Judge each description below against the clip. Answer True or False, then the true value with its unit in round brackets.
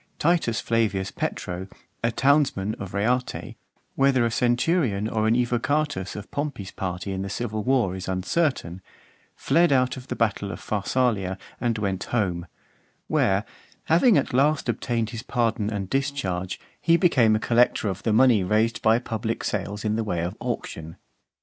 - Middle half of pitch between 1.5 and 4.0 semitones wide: False (4.6 semitones)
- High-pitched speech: False (110 Hz)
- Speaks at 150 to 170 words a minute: True (160 wpm)